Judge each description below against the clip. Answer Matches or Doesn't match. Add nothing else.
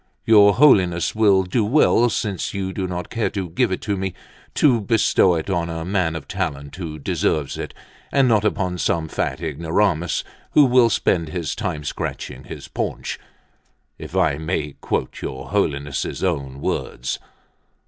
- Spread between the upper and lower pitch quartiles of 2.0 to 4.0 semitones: Doesn't match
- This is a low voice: Matches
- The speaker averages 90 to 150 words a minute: Doesn't match